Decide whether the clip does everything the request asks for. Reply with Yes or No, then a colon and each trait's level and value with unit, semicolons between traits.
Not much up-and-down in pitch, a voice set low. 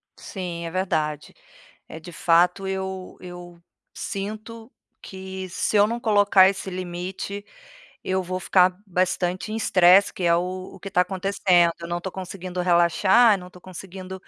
No: narrow, 1.6 semitones; medium, 185 Hz